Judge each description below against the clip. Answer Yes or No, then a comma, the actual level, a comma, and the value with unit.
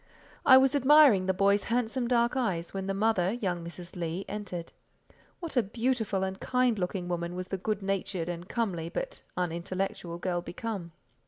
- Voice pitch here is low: No, high, 195 Hz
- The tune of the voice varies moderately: Yes, average, 4.6 semitones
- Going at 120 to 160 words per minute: No, average, 170 wpm